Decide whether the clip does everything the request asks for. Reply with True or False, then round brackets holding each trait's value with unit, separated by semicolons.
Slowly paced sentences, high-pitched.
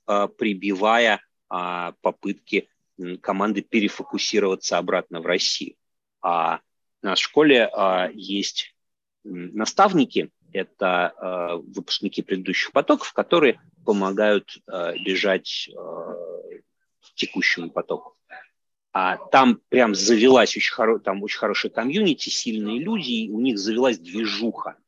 False (95 wpm; 105 Hz)